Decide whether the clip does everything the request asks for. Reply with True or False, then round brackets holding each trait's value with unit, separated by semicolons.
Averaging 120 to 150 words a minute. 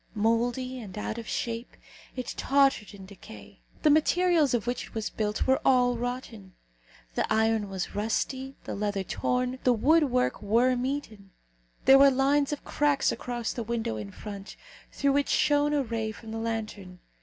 False (170 wpm)